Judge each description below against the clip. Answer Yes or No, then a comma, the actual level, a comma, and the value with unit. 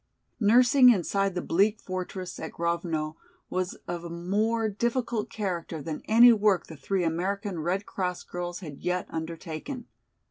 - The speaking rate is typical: Yes, average, 145 wpm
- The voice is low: No, medium, 185 Hz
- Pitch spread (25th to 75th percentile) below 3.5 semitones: No, average, 3.8 semitones